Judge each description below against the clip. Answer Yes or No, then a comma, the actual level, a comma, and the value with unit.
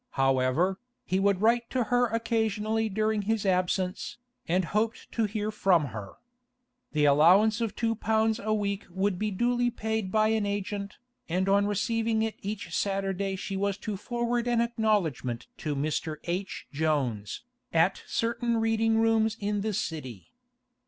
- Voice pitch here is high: Yes, high, 205 Hz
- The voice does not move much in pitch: No, average, 3.4 semitones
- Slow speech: No, average, 150 wpm